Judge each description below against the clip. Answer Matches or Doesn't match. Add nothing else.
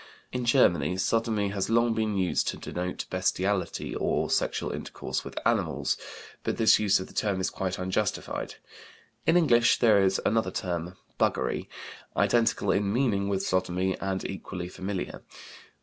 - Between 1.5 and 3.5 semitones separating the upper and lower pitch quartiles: Matches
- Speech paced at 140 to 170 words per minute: Matches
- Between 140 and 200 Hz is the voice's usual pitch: Doesn't match